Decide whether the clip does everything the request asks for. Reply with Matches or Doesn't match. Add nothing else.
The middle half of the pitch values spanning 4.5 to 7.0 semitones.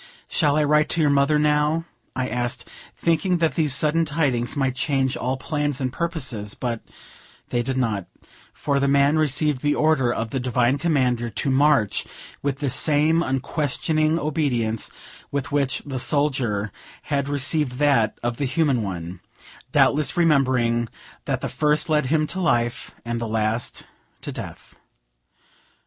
Doesn't match